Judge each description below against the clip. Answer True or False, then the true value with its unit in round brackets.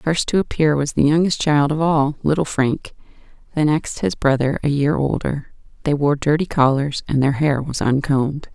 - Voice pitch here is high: False (145 Hz)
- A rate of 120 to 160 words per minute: False (195 wpm)